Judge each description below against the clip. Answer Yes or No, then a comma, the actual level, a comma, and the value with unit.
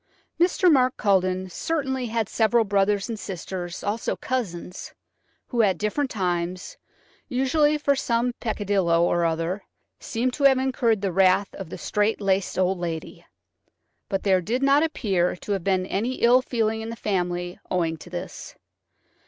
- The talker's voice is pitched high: Yes, high, 205 Hz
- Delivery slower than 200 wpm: Yes, average, 150 wpm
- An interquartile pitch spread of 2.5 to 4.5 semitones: No, average, 5.2 semitones